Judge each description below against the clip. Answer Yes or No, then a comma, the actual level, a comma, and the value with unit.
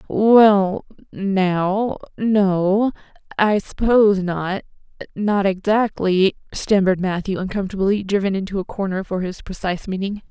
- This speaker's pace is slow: Yes, slow, 105 wpm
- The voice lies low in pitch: No, high, 195 Hz